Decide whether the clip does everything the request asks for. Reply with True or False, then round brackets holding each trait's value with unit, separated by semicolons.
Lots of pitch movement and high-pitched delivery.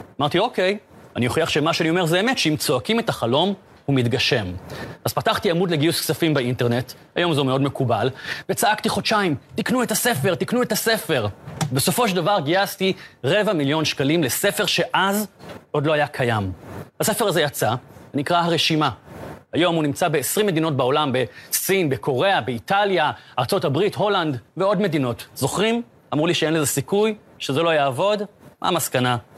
False (6.1 semitones; 160 Hz)